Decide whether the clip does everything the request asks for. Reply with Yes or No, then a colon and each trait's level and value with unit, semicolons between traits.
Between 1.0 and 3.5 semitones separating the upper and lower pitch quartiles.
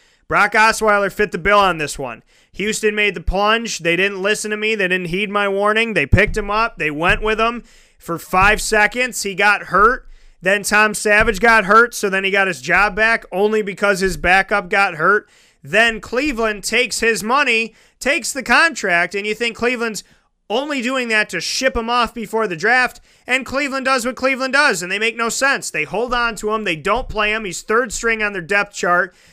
Yes: average, 2.8 semitones